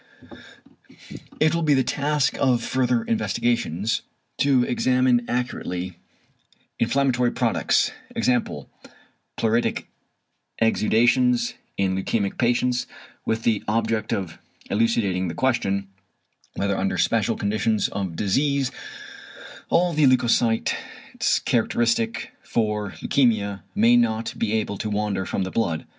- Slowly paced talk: Yes, slow, 110 wpm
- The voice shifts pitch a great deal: No, average, 3.5 semitones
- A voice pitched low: Yes, low, 115 Hz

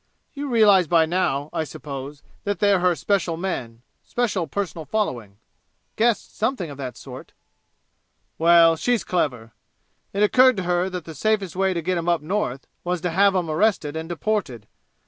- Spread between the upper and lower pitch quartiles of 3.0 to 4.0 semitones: No, average, 4.5 semitones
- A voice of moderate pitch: Yes, medium, 175 Hz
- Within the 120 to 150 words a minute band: No, average, 165 wpm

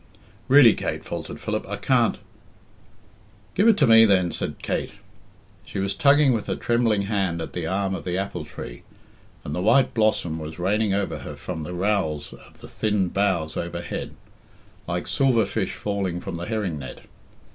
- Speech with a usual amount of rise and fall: Yes, average, 3.9 semitones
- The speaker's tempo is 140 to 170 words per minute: No, average, 180 wpm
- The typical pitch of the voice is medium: No, low, 100 Hz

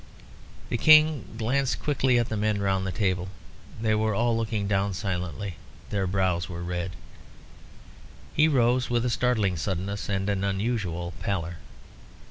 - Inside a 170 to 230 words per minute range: No, average, 145 wpm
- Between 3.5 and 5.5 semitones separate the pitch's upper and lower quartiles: Yes, average, 4.1 semitones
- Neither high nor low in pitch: No, low, 100 Hz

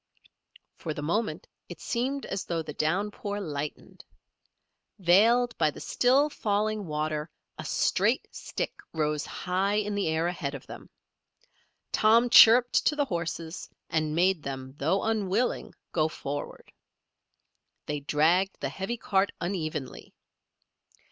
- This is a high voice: No, medium, 180 Hz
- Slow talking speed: Yes, slow, 130 wpm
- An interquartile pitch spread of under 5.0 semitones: No, wide, 5.6 semitones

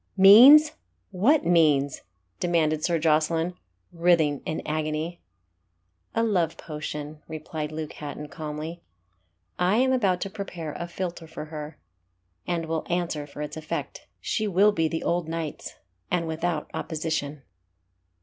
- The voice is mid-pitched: Yes, medium, 165 Hz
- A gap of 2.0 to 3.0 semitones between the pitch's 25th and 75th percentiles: Yes, narrow, 2.6 semitones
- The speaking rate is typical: No, slow, 130 wpm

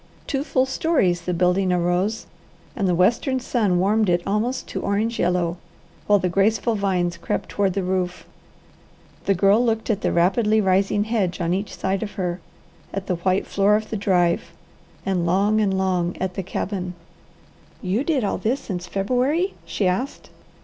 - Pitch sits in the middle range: No, high, 195 Hz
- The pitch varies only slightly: No, average, 3.2 semitones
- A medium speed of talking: Yes, average, 170 wpm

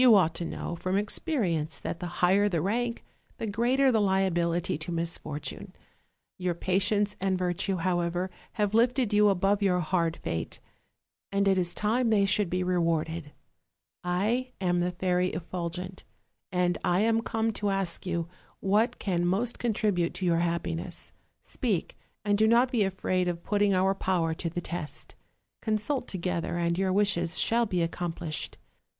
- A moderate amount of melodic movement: Yes, average, 3.2 semitones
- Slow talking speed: No, average, 160 wpm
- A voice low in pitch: No, medium, 185 Hz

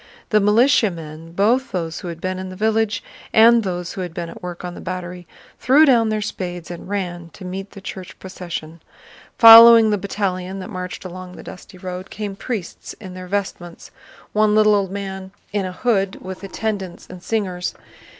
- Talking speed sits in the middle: Yes, average, 180 wpm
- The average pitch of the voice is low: No, high, 190 Hz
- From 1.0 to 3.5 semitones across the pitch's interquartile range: Yes, average, 2.8 semitones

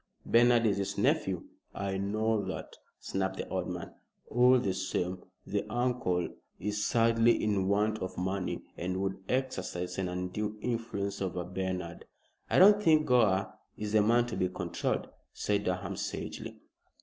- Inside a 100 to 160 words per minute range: Yes, average, 150 wpm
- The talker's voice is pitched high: No, low, 100 Hz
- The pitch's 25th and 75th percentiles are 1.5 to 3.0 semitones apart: No, average, 3.6 semitones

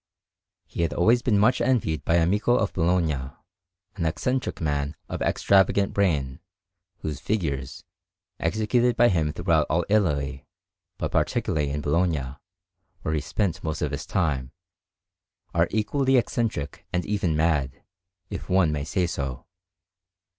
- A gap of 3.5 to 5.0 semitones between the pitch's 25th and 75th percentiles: No, wide, 5.6 semitones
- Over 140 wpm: No, slow, 135 wpm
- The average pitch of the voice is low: Yes, very low, 85 Hz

